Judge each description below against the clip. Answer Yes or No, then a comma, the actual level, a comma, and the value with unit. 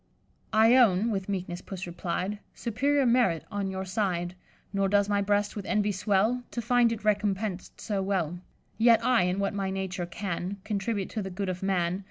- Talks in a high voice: Yes, high, 200 Hz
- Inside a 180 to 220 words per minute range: Yes, average, 185 wpm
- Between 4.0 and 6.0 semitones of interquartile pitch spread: No, narrow, 2.5 semitones